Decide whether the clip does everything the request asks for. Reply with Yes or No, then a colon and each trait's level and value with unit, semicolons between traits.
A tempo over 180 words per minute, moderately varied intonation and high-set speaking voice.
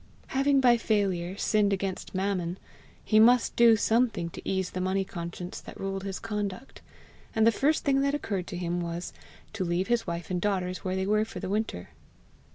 Yes: average, 190 wpm; average, 3.7 semitones; high, 195 Hz